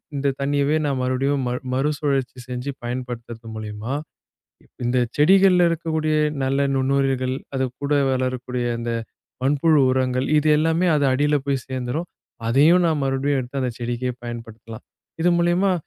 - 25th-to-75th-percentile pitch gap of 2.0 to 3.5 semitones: Yes, average, 2.8 semitones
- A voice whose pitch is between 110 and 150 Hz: Yes, low, 135 Hz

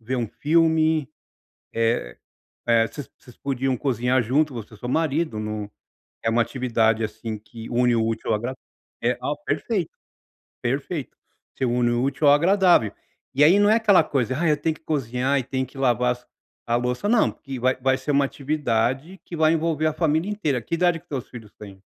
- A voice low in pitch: Yes, low, 130 Hz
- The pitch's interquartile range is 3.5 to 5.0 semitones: Yes, average, 4.7 semitones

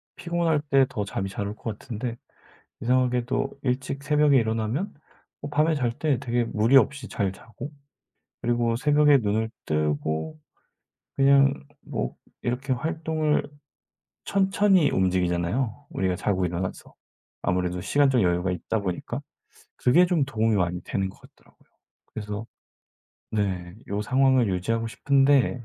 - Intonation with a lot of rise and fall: Yes, wide, 5.8 semitones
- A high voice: No, low, 120 Hz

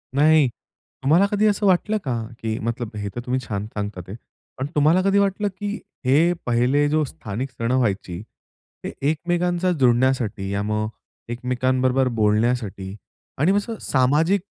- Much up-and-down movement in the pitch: Yes, wide, 6.6 semitones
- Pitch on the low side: Yes, low, 130 Hz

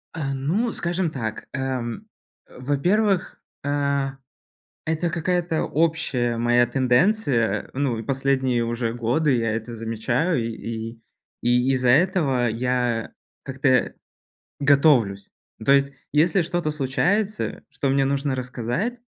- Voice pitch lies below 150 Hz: Yes, low, 135 Hz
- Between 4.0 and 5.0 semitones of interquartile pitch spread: Yes, average, 4.7 semitones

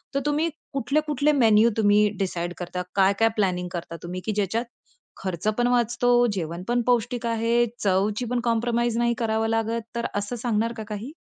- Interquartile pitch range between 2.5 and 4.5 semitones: Yes, average, 3.2 semitones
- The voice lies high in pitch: Yes, high, 225 Hz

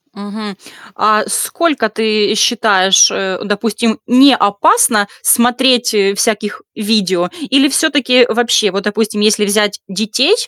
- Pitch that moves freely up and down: No, average, 3.0 semitones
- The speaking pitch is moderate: No, high, 215 Hz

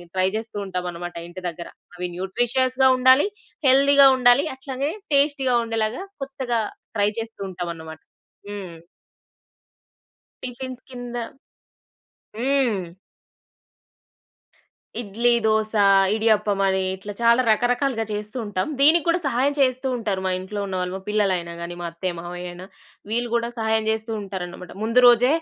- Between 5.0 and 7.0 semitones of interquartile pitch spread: Yes, average, 5.3 semitones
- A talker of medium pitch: No, high, 220 Hz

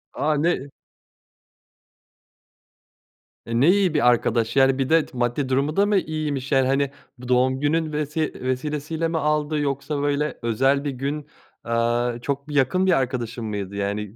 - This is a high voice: No, medium, 140 Hz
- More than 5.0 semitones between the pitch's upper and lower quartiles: No, average, 3.5 semitones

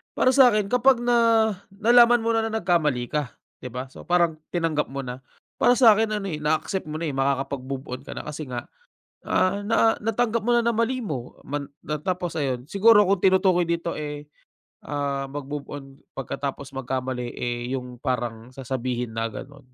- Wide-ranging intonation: Yes, wide, 8.2 semitones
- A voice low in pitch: No, medium, 150 Hz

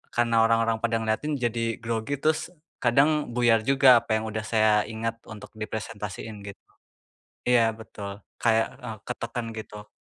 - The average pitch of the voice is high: No, low, 115 Hz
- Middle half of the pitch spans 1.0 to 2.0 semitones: Yes, narrow, 1.6 semitones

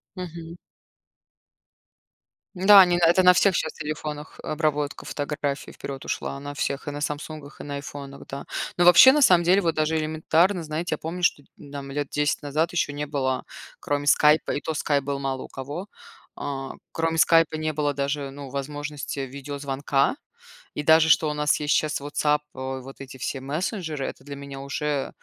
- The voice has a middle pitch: Yes, medium, 150 Hz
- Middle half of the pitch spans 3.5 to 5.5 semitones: No, narrow, 2.4 semitones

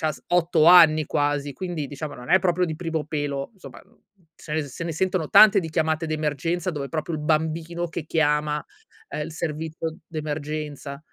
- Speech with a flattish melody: Yes, narrow, 2.0 semitones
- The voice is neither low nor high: Yes, medium, 155 Hz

